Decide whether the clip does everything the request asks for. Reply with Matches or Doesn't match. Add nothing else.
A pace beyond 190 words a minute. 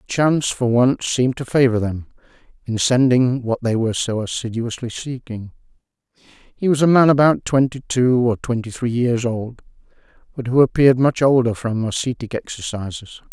Doesn't match